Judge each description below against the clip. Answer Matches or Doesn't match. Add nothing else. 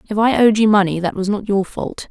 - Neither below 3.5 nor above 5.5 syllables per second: Doesn't match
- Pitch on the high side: Matches